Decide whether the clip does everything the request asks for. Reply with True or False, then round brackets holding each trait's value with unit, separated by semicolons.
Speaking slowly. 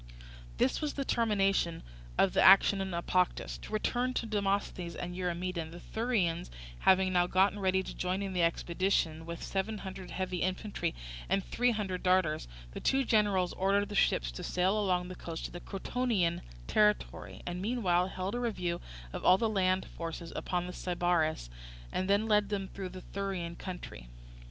False (175 wpm)